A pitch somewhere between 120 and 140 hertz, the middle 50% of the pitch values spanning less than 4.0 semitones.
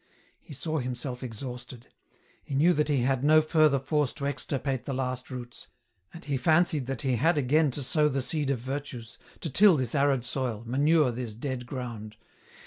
Yes: low, 135 Hz; average, 3.2 semitones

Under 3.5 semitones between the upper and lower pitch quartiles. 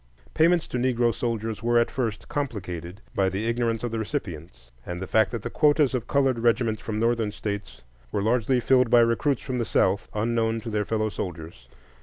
Yes: average, 3.0 semitones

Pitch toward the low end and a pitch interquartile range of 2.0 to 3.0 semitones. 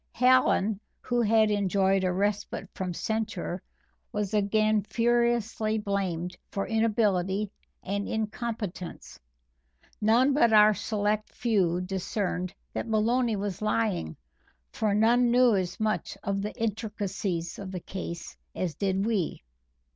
No: high, 210 Hz; average, 2.7 semitones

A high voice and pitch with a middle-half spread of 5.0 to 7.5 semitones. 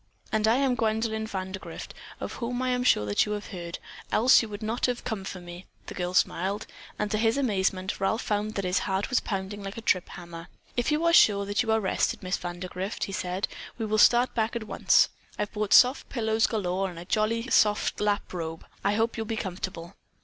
No: high, 210 Hz; average, 3.1 semitones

